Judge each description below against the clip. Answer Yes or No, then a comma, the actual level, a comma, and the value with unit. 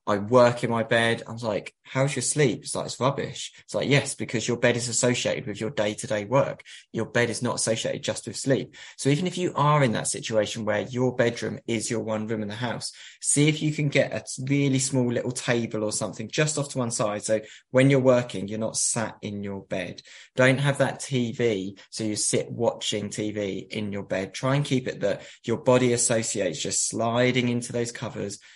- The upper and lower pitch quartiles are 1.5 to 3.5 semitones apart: Yes, average, 3.2 semitones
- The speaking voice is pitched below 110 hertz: No, low, 120 Hz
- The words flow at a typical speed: No, fast, 220 wpm